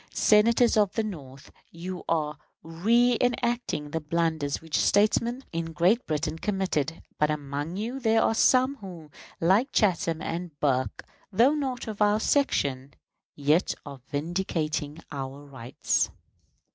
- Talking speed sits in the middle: No, slow, 130 wpm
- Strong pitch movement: Yes, wide, 6.6 semitones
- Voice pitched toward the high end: No, medium, 170 Hz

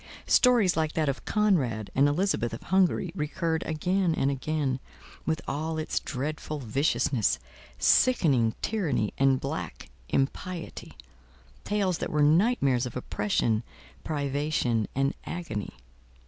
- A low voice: No, medium, 150 Hz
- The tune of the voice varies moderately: Yes, average, 4.9 semitones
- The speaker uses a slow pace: Yes, slow, 120 wpm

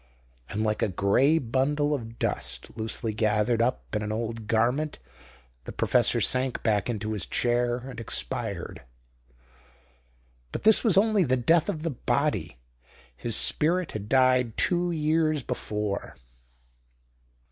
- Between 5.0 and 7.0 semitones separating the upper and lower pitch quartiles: Yes, wide, 5.6 semitones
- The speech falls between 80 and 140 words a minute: Yes, slow, 135 wpm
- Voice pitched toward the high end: No, low, 120 Hz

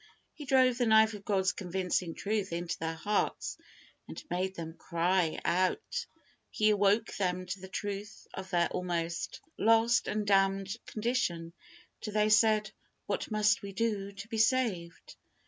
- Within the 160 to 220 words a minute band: No, average, 150 wpm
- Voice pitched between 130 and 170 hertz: No, high, 200 Hz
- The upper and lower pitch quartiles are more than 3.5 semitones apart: No, average, 3.2 semitones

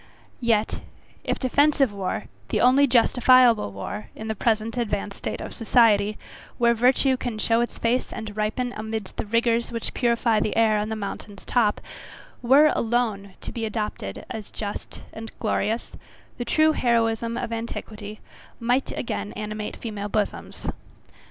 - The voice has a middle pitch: No, high, 225 Hz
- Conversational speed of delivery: Yes, average, 150 wpm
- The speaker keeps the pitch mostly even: Yes, narrow, 2.3 semitones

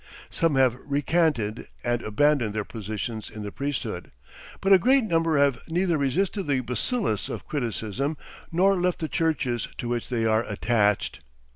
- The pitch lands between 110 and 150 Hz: Yes, low, 135 Hz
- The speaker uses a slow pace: No, average, 155 wpm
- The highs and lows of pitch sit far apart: Yes, wide, 6.5 semitones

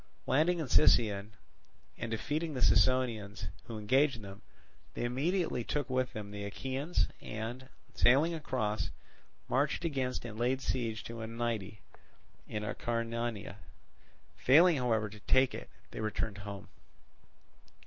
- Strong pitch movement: No, average, 3.7 semitones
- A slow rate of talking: Yes, slow, 125 wpm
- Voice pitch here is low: Yes, low, 120 Hz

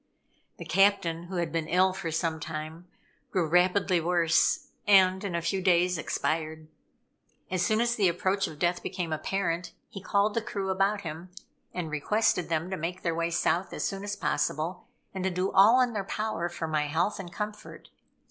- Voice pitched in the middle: Yes, medium, 180 Hz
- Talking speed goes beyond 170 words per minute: Yes, average, 185 wpm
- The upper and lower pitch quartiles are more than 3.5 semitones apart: No, average, 2.8 semitones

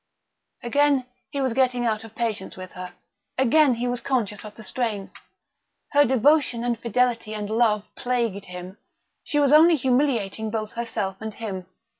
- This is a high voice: Yes, high, 235 Hz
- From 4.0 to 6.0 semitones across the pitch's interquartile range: No, average, 3.4 semitones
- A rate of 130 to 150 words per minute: No, average, 160 wpm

